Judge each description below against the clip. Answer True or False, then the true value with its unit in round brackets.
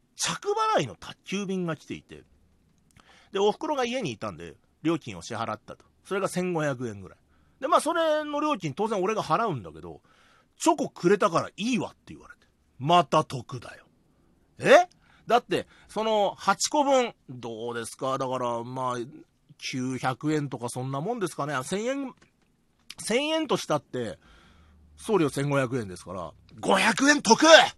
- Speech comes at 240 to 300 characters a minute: True (270 characters per minute)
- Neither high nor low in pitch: True (150 Hz)